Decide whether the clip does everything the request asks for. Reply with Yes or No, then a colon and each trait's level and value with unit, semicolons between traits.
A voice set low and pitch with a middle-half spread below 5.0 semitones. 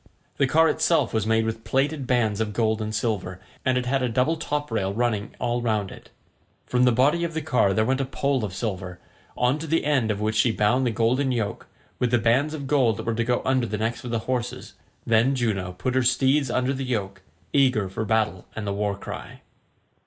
Yes: low, 120 Hz; average, 3.4 semitones